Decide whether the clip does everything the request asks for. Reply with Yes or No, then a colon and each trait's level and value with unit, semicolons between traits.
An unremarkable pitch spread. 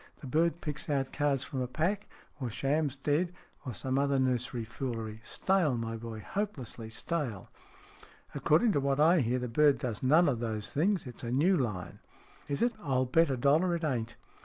Yes: average, 4.5 semitones